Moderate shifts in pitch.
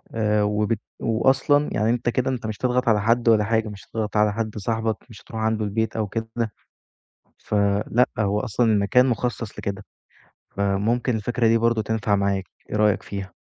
No: narrow, 1.9 semitones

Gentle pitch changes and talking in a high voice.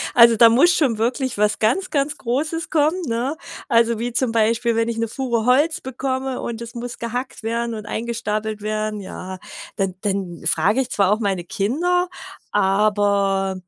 No: average, 3.6 semitones; high, 230 Hz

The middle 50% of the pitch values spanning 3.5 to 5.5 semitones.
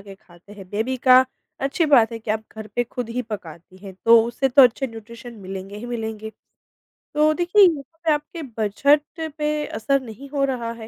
Yes: average, 4.4 semitones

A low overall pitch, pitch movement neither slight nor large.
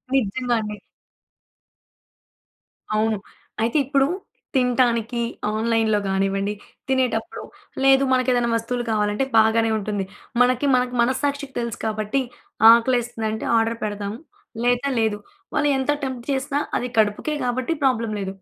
No: high, 235 Hz; average, 3.0 semitones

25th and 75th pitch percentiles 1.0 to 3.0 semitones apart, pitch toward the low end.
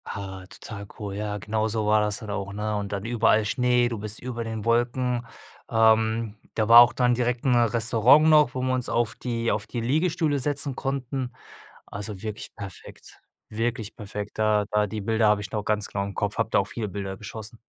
Yes: narrow, 2.6 semitones; low, 110 Hz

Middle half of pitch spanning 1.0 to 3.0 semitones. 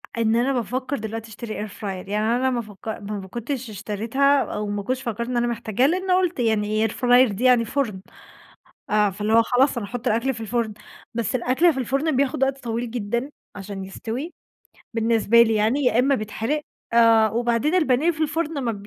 No: average, 3.4 semitones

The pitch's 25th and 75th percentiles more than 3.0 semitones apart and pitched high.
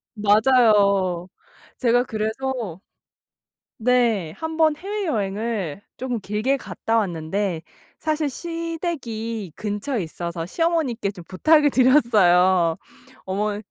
Yes: wide, 5.6 semitones; high, 220 Hz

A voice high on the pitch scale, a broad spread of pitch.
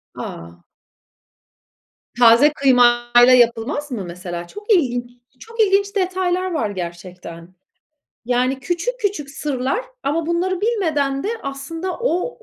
Yes: very high, 275 Hz; wide, 7.5 semitones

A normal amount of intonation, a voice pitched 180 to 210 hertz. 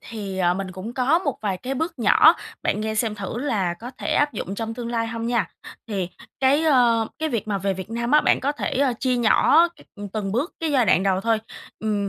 No: average, 4.7 semitones; high, 230 Hz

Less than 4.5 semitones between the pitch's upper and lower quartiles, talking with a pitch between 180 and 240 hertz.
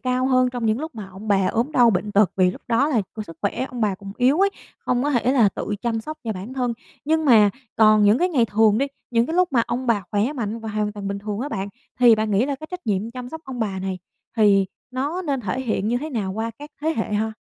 Yes: average, 3.9 semitones; high, 230 Hz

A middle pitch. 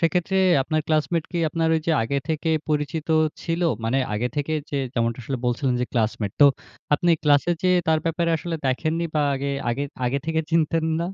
Yes: medium, 155 Hz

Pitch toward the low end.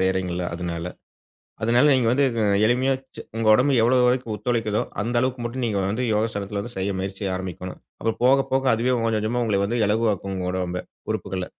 Yes: low, 110 Hz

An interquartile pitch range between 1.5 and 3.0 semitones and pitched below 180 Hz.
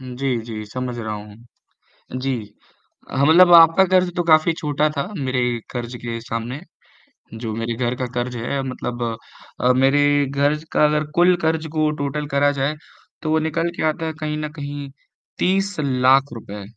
No: average, 4.1 semitones; medium, 140 Hz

